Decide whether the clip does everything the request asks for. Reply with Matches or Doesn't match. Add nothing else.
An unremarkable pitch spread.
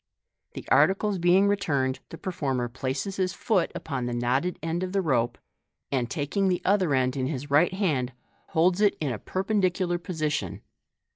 Doesn't match